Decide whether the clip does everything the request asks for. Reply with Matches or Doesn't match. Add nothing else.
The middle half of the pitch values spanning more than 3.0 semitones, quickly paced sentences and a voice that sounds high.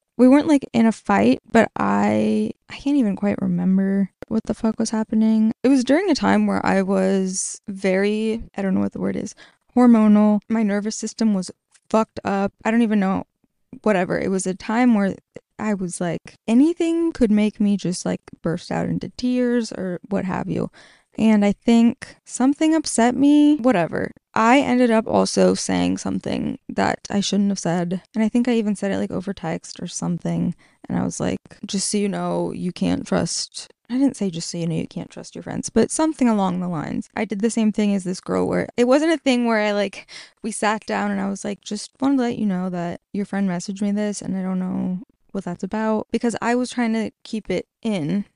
Matches